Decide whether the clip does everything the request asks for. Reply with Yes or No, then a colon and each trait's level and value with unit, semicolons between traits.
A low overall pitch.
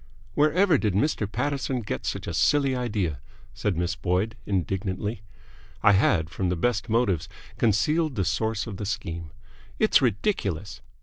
Yes: low, 105 Hz